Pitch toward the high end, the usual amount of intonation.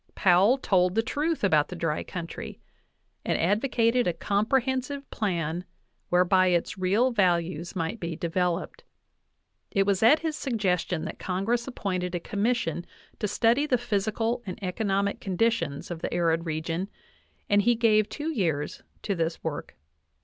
Yes: high, 195 Hz; average, 5.0 semitones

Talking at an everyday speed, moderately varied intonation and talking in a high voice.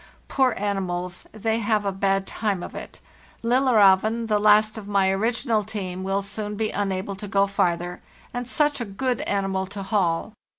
No: average, 170 wpm; narrow, 2.3 semitones; high, 205 Hz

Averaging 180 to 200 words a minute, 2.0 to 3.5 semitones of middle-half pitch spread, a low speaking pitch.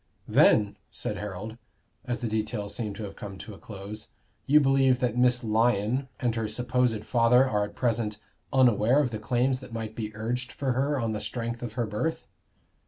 Yes: average, 190 wpm; average, 2.8 semitones; low, 115 Hz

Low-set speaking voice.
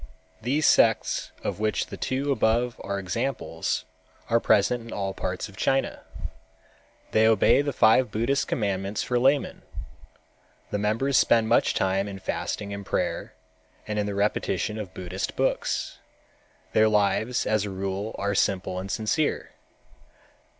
Yes: low, 105 Hz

